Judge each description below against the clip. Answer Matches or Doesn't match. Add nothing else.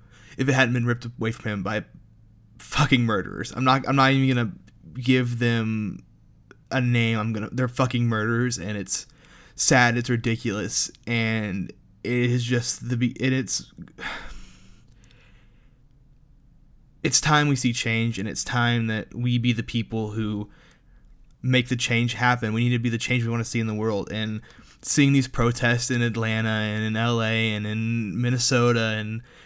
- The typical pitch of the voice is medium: Doesn't match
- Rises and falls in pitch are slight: Matches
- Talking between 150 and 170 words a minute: Matches